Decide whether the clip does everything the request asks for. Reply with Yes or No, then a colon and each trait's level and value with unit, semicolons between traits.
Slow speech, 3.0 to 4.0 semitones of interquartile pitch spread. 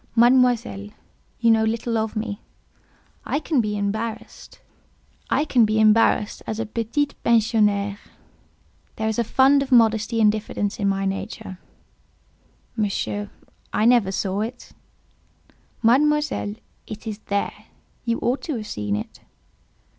No: slow, 120 wpm; narrow, 2.4 semitones